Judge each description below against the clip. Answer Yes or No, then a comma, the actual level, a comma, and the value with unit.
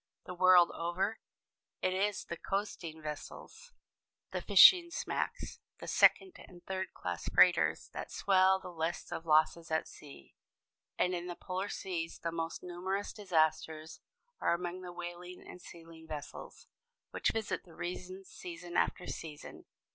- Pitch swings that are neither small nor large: No, narrow, 2.2 semitones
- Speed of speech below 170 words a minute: Yes, average, 145 wpm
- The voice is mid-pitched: Yes, medium, 175 Hz